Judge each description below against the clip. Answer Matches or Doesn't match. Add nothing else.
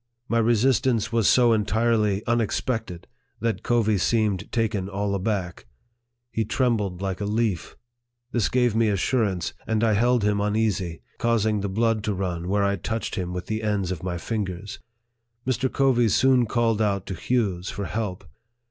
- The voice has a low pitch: Matches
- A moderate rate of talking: Matches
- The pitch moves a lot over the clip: Doesn't match